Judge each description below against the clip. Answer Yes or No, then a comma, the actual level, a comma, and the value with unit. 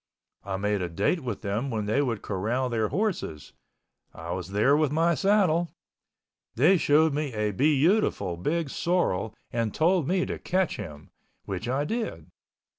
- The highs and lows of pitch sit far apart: Yes, wide, 8.4 semitones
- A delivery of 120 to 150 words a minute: No, average, 160 wpm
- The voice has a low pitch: Yes, low, 130 Hz